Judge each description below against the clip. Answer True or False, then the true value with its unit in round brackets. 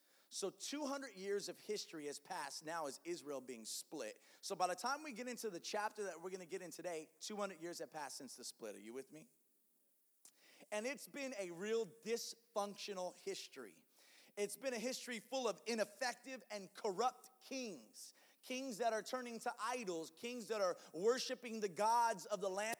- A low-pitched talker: False (220 Hz)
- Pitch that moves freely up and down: False (4.9 semitones)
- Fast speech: False (190 wpm)